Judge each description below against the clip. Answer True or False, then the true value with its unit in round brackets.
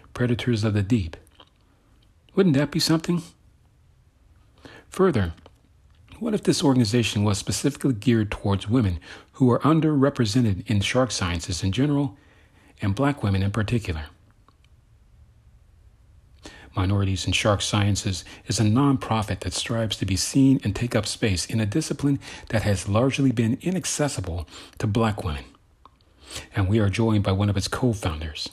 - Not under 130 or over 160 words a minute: True (145 wpm)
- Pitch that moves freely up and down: False (5.0 semitones)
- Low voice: True (110 Hz)